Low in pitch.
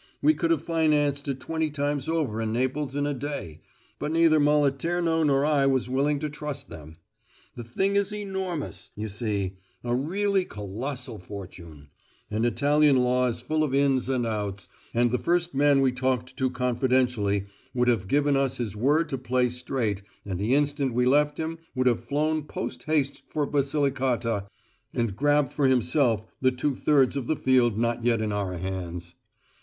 Yes: low, 130 Hz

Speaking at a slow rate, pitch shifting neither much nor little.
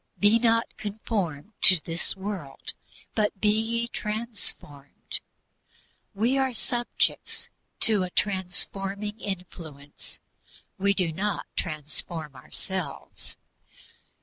Yes: slow, 90 wpm; average, 4.3 semitones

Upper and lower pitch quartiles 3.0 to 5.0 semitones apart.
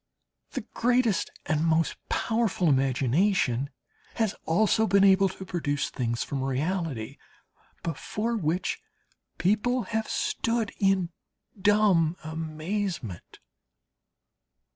No: wide, 5.4 semitones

